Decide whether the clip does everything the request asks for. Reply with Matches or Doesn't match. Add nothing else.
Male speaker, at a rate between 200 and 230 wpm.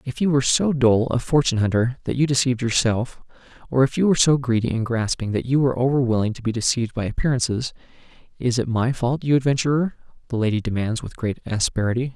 Matches